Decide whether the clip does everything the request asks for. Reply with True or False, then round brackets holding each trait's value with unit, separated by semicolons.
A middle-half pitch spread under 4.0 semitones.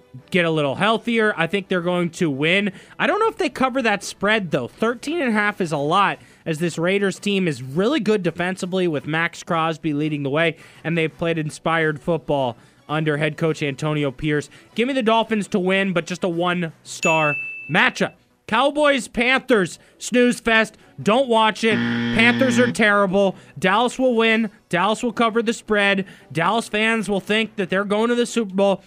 False (5.5 semitones)